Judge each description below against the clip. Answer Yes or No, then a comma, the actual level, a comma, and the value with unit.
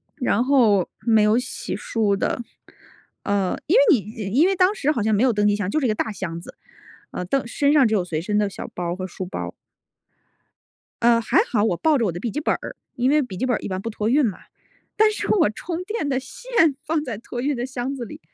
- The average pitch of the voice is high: Yes, high, 230 Hz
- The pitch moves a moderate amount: No, wide, 5.8 semitones